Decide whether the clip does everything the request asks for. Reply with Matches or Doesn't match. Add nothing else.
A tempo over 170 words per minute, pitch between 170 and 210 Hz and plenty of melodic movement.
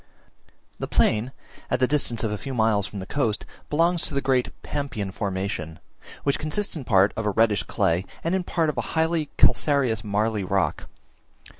Doesn't match